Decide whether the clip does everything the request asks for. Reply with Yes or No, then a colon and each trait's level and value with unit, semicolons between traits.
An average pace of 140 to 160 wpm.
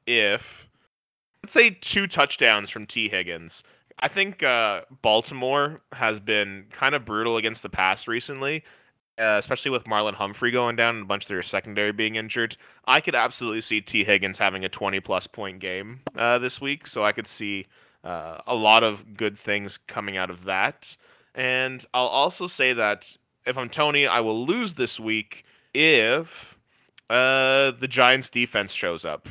No: average, 175 wpm